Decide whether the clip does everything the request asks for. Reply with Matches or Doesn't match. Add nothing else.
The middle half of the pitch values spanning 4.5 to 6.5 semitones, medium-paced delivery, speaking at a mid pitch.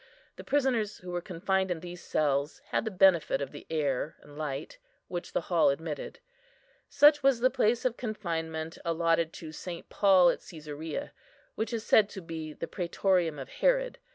Matches